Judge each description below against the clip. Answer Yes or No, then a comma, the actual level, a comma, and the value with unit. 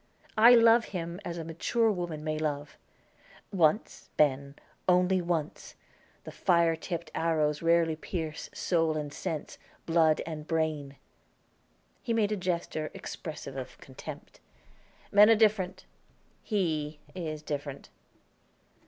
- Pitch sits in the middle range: Yes, medium, 165 Hz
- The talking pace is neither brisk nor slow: No, slow, 120 wpm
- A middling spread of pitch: Yes, average, 3.2 semitones